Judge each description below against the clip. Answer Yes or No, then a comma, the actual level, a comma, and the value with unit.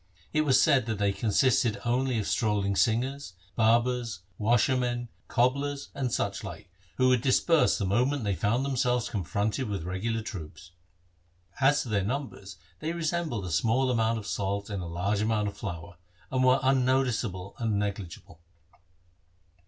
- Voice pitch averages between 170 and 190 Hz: No, low, 115 Hz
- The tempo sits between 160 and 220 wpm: No, average, 150 wpm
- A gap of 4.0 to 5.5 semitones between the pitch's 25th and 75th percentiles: Yes, average, 4.3 semitones